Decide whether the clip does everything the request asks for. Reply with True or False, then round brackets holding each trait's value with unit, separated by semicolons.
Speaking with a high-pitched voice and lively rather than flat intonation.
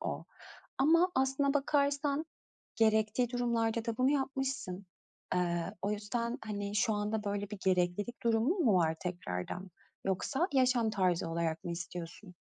True (220 Hz; 6.1 semitones)